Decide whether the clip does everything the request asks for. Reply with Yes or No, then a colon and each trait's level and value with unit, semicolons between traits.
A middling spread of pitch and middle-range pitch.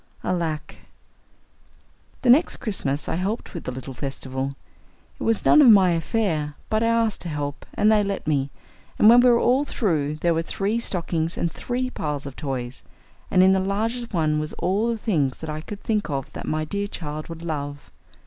No: wide, 6.4 semitones; medium, 170 Hz